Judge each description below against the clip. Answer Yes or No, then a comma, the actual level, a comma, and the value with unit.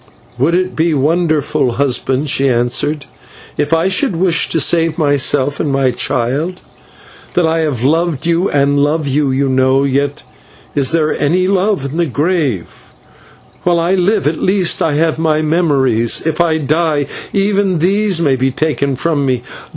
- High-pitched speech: No, medium, 155 Hz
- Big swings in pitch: No, average, 3.7 semitones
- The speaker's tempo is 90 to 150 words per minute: No, average, 165 wpm